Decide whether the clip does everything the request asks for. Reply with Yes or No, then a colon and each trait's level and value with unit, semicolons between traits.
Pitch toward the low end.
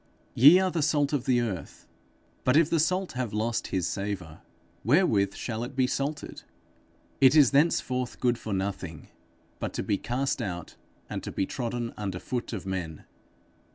Yes: low, 120 Hz